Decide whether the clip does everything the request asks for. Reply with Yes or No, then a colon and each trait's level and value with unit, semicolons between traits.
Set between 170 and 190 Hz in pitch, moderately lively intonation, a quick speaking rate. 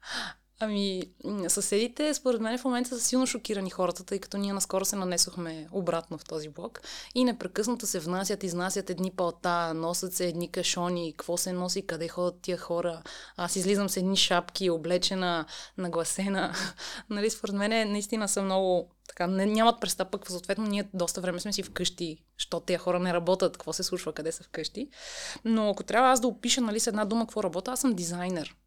Yes: medium, 185 Hz; average, 3.1 semitones; fast, 180 wpm